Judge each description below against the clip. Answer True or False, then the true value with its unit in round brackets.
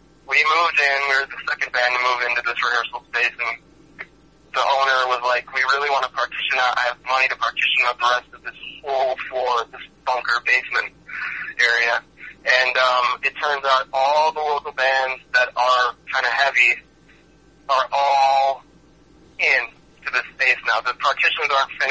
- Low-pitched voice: True (130 Hz)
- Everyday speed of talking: True (175 wpm)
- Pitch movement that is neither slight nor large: False (2.0 semitones)